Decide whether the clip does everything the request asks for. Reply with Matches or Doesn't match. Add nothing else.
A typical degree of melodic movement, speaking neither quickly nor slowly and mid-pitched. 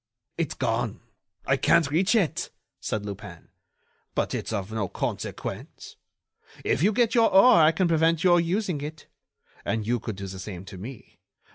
Doesn't match